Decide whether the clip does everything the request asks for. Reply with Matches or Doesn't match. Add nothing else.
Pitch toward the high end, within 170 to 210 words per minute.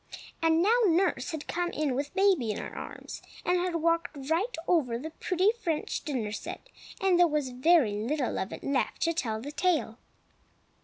Matches